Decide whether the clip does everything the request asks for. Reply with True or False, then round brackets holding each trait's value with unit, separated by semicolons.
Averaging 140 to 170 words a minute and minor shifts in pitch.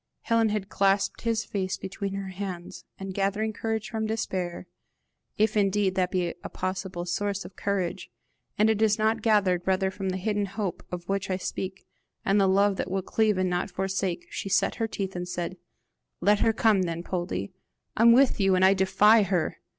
False (190 wpm; 2.1 semitones)